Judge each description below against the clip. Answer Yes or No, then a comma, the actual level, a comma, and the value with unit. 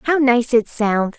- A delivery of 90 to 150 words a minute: No, fast, 205 wpm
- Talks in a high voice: Yes, high, 240 Hz